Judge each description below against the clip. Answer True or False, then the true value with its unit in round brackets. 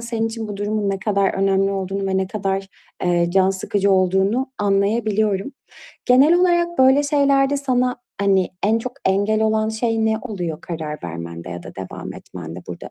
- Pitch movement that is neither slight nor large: True (3.4 semitones)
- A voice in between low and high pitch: False (200 Hz)